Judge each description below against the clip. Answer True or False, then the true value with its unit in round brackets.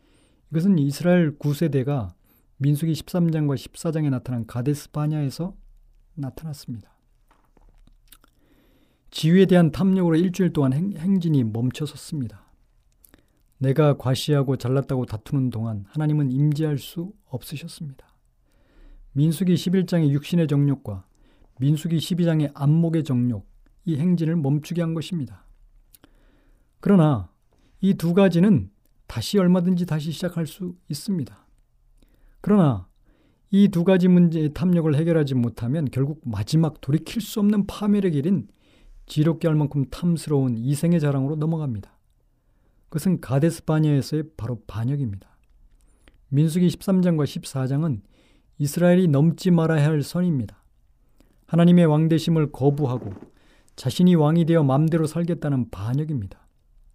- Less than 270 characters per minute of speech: False (290 characters per minute)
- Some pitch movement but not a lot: True (4.4 semitones)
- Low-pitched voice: False (150 Hz)